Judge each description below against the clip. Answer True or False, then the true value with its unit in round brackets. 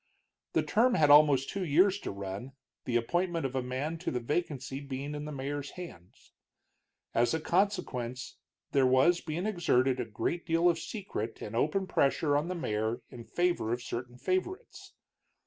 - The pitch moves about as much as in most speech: False (5.8 semitones)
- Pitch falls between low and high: True (145 Hz)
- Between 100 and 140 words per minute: False (170 wpm)